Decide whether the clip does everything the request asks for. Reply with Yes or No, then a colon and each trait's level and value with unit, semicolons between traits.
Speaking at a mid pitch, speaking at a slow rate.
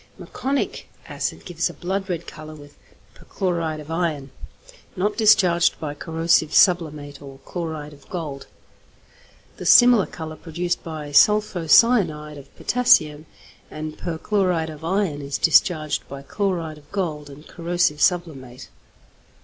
Yes: medium, 160 Hz; slow, 130 wpm